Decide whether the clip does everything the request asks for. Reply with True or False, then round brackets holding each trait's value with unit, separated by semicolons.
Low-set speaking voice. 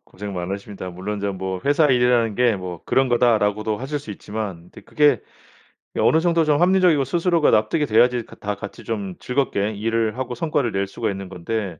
True (110 Hz)